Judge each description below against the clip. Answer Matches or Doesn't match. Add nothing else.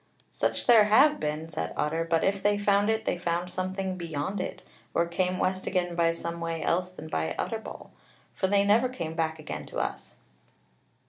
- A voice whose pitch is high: Doesn't match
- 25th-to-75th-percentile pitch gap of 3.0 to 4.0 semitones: Matches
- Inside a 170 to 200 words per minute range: Matches